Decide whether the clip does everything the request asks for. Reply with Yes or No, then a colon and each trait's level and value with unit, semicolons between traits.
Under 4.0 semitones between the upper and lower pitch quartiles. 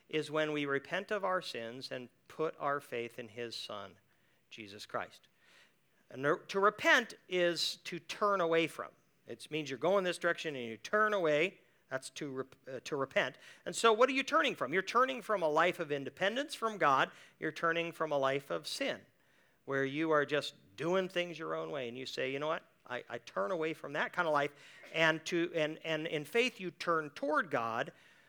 No: average, 4.3 semitones